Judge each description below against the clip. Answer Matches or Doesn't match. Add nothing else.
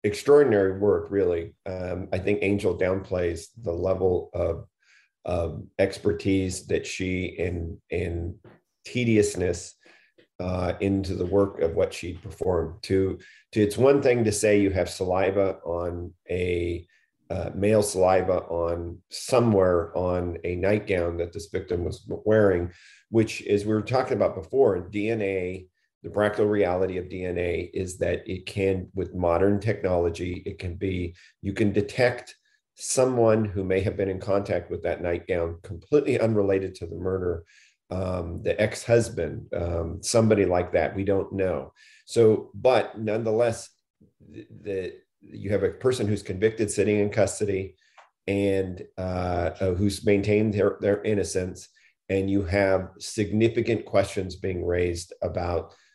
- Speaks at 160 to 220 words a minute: Doesn't match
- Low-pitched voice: Matches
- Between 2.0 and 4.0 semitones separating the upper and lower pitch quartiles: Matches